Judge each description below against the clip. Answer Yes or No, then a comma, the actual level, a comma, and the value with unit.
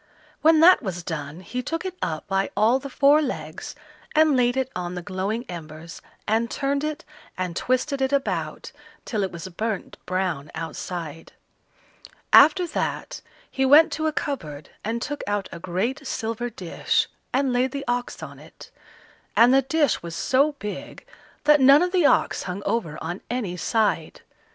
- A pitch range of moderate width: No, wide, 7.5 semitones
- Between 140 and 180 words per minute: Yes, average, 170 wpm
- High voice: Yes, high, 235 Hz